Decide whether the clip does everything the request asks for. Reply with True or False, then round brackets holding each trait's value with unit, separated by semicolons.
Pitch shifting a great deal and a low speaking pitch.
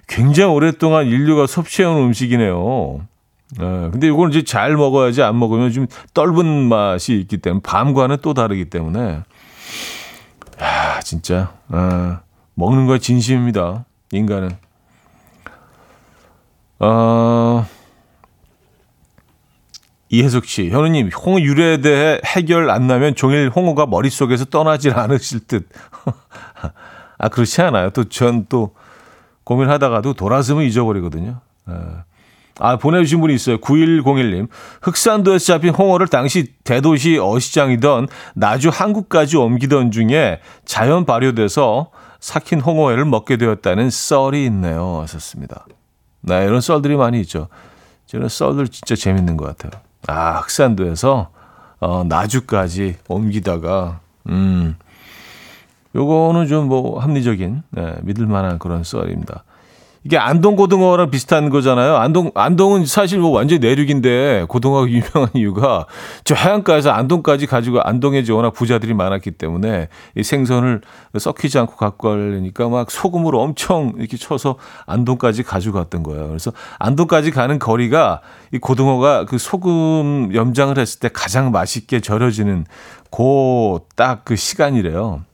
True (6.1 semitones; 125 Hz)